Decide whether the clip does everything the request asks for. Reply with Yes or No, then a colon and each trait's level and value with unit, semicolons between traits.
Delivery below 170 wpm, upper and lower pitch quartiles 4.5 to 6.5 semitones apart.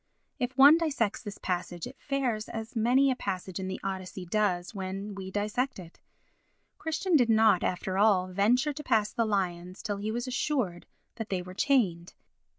No: average, 175 wpm; average, 4.9 semitones